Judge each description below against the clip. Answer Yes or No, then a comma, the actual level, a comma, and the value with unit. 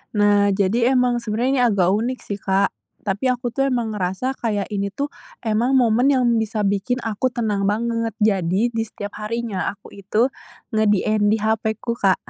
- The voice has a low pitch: No, high, 220 Hz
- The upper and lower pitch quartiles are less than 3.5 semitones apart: Yes, average, 2.9 semitones